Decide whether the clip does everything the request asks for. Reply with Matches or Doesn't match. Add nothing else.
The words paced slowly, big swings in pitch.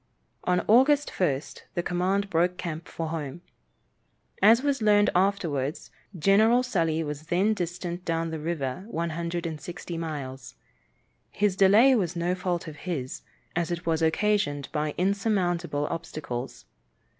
Doesn't match